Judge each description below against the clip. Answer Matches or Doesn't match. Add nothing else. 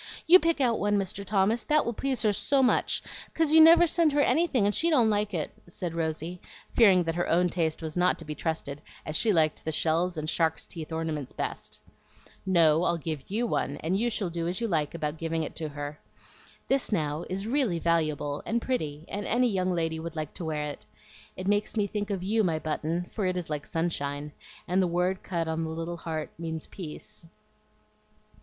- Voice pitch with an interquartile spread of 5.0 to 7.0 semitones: Doesn't match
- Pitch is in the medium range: Matches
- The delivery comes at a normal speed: Doesn't match